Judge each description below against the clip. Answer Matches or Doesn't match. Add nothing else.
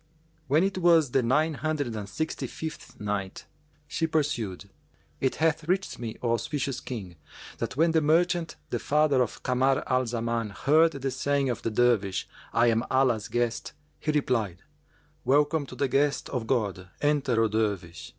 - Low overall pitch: Matches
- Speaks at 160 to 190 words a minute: Matches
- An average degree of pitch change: Matches